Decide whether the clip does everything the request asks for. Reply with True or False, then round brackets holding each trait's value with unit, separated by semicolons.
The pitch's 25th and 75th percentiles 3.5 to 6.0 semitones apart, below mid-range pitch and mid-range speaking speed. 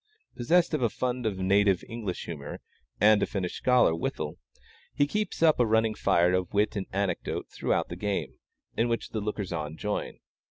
True (4.3 semitones; 105 Hz; 185 wpm)